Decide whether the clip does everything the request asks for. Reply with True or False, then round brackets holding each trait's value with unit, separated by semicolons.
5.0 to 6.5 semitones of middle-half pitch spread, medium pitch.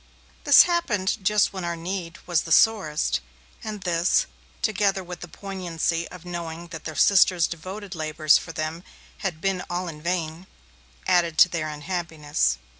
False (2.7 semitones; 175 Hz)